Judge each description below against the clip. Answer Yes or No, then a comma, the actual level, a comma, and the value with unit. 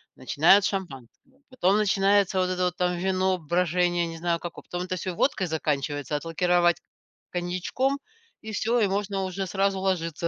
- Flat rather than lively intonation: Yes, narrow, 2.2 semitones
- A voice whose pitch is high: No, medium, 180 Hz